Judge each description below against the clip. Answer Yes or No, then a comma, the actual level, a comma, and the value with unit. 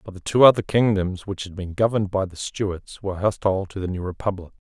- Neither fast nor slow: No, fast, 230 wpm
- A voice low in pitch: Yes, very low, 95 Hz